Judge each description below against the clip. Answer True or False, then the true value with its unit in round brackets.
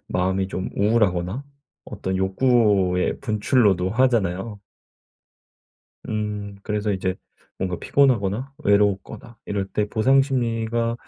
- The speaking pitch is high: False (105 Hz)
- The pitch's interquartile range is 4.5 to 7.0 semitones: False (3.6 semitones)